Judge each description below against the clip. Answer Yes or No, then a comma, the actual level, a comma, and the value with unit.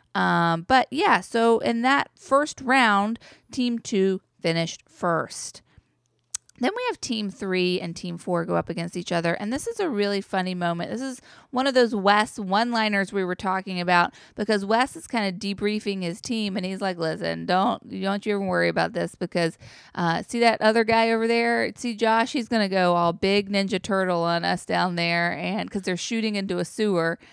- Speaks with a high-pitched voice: Yes, high, 200 Hz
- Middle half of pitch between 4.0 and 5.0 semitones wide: Yes, average, 4.4 semitones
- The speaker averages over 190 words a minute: Yes, average, 200 wpm